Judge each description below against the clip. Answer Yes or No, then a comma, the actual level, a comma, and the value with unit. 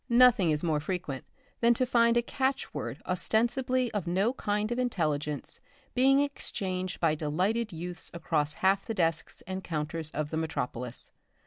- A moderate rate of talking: Yes, average, 155 wpm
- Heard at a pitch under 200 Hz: Yes, medium, 185 Hz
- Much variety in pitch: Yes, wide, 6.8 semitones